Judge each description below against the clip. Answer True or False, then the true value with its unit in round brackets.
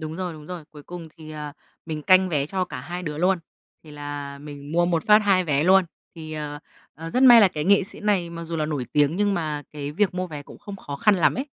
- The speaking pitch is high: False (165 Hz)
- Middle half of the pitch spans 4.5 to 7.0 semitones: False (3.8 semitones)